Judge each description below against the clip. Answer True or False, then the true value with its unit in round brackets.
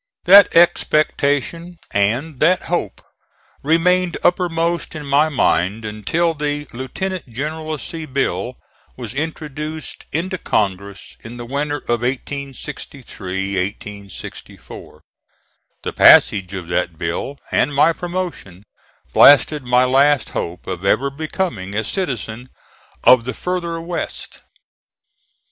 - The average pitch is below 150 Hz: True (140 Hz)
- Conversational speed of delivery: False (110 wpm)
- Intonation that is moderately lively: False (7.0 semitones)